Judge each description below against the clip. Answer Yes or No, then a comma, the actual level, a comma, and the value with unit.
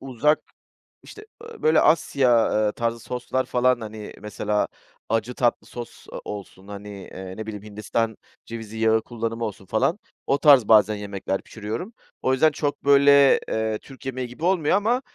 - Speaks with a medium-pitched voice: No, low, 115 Hz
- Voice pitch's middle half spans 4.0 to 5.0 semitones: Yes, average, 4.5 semitones